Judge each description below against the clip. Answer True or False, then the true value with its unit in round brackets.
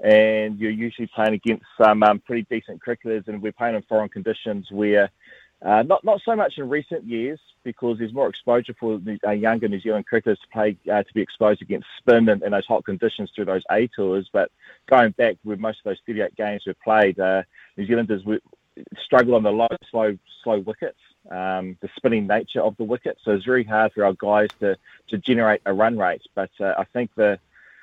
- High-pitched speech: False (110 Hz)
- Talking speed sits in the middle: False (210 wpm)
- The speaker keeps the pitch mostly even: True (2.0 semitones)